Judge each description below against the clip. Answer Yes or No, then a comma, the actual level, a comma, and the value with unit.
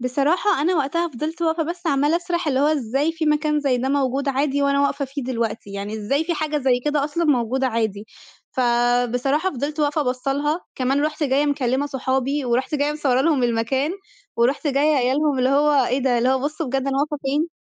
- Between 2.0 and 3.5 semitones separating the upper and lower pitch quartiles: Yes, average, 2.9 semitones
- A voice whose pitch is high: Yes, very high, 280 Hz